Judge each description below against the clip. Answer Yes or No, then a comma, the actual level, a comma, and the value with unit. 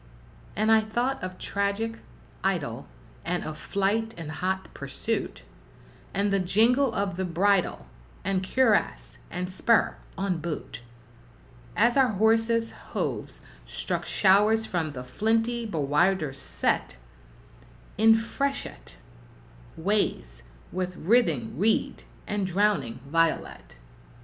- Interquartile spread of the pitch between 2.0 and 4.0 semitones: No, average, 4.7 semitones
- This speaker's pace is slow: Yes, slow, 110 wpm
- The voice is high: Yes, high, 195 Hz